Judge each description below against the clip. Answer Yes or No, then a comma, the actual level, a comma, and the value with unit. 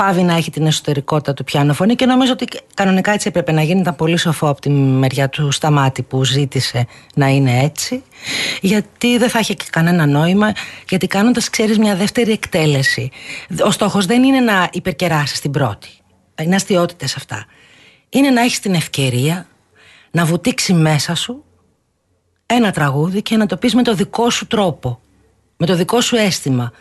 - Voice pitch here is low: No, medium, 170 Hz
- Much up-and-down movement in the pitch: Yes, wide, 7.3 semitones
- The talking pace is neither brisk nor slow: No, fast, 175 wpm